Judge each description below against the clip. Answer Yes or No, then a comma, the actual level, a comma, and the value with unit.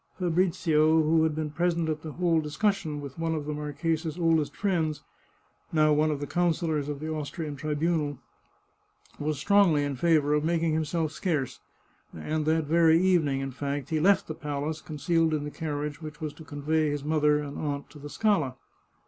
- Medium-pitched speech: Yes, medium, 155 Hz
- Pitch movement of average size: No, narrow, 1.9 semitones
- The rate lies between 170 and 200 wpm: Yes, average, 180 wpm